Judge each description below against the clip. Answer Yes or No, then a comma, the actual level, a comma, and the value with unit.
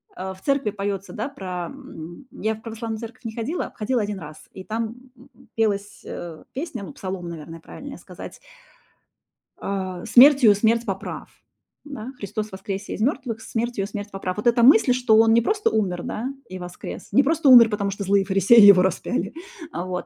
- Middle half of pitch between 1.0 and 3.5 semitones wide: No, average, 4.0 semitones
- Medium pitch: No, high, 215 Hz